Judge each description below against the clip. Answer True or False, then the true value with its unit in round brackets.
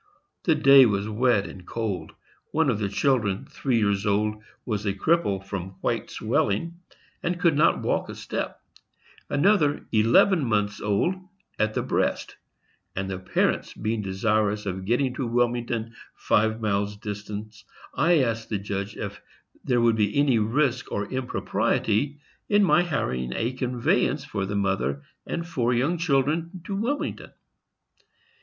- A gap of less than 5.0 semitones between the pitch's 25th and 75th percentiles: False (5.3 semitones)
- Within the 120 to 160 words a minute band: True (150 wpm)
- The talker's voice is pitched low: True (115 Hz)